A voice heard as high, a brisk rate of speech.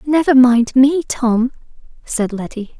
No: very high, 255 Hz; slow, 130 wpm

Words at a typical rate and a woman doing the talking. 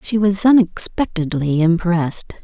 No: slow, 100 wpm; female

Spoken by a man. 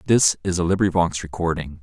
Yes: male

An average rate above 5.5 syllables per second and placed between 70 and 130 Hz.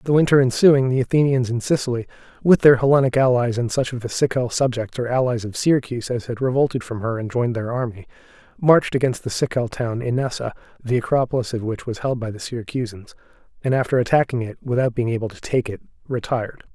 Yes: 6.4 syllables/s; low, 125 Hz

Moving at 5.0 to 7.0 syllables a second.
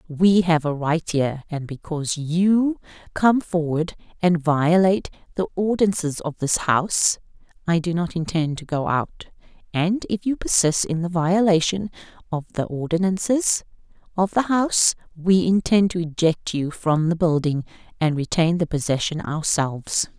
No: 4.6 syllables/s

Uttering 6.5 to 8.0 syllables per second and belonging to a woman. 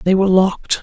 Yes: 7.0 syllables/s; female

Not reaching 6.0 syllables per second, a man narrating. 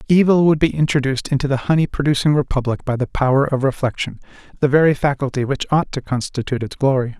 No: 6.6 syllables/s; male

